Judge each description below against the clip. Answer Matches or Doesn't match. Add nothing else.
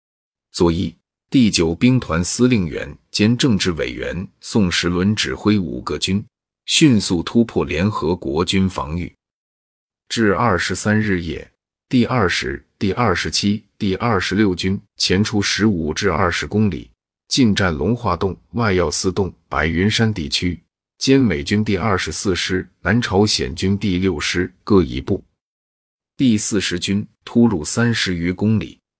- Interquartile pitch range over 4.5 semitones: Doesn't match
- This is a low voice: Matches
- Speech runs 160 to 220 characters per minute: Matches